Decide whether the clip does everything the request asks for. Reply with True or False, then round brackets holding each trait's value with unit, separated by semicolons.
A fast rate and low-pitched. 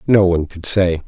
True (225 wpm; 90 Hz)